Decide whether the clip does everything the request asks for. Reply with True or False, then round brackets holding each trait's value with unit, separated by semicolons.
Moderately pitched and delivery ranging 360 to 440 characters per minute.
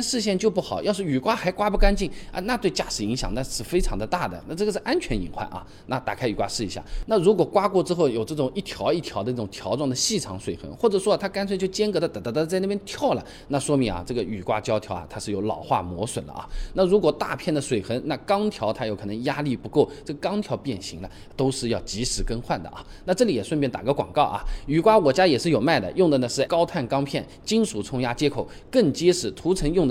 True (145 Hz; 370 characters per minute)